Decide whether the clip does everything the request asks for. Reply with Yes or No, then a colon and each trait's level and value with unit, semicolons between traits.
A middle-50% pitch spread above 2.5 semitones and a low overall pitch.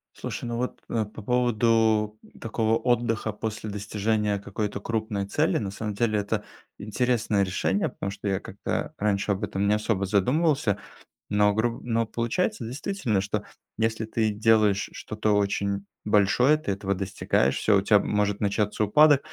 No: narrow, 2.2 semitones; low, 105 Hz